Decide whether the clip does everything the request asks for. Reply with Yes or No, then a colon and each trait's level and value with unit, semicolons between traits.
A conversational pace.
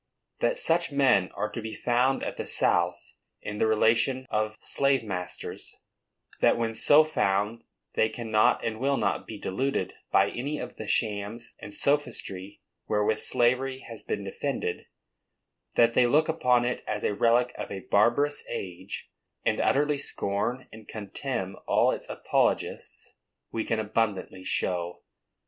Yes: average, 150 wpm